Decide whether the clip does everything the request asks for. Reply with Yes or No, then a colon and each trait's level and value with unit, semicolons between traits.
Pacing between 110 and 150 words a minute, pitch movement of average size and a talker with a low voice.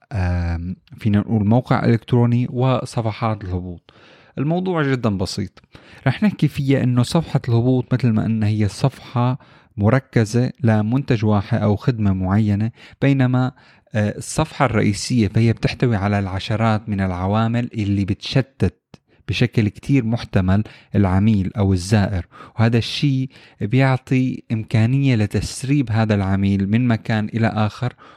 Yes: average, 115 wpm; average, 3.7 semitones; low, 115 Hz